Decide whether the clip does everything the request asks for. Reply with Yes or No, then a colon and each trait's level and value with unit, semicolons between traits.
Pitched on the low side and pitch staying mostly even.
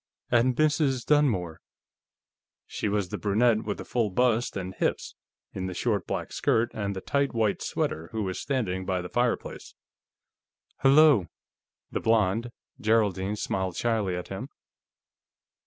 No: low, 110 Hz; average, 4.5 semitones